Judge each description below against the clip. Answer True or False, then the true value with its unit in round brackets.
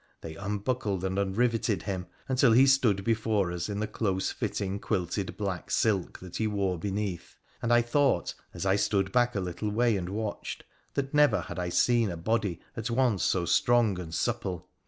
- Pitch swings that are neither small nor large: True (3.7 semitones)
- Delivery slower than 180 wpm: False (185 wpm)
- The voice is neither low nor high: False (100 Hz)